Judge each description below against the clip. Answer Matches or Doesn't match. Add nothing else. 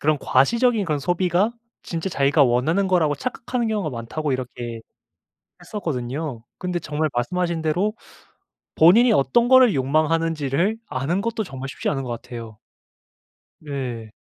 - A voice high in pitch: Doesn't match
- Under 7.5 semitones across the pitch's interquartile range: Matches